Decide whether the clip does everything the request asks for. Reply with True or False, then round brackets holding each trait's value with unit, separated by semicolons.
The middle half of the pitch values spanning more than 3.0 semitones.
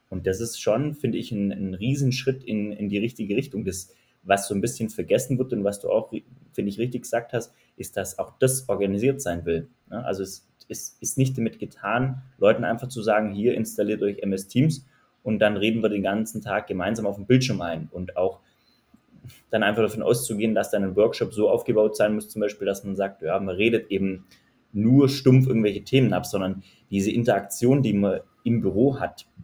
True (3.6 semitones)